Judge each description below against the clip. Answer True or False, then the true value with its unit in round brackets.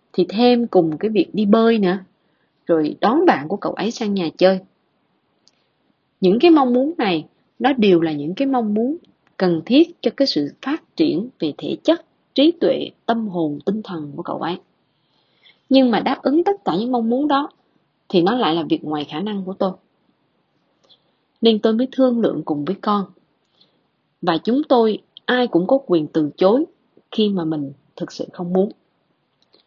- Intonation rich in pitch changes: True (7.2 semitones)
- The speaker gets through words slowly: False (185 wpm)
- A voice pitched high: True (210 Hz)